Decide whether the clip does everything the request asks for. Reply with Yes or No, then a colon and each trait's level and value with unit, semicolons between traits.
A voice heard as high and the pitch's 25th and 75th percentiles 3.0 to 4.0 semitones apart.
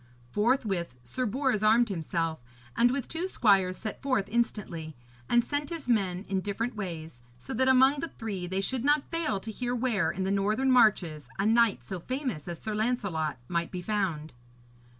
No: high, 210 Hz; wide, 5.6 semitones